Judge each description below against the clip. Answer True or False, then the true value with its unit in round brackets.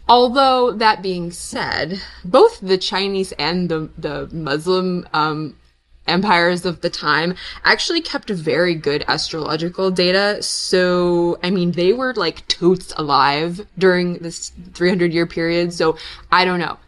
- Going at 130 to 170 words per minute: True (140 wpm)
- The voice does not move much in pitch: True (2.2 semitones)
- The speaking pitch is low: False (180 Hz)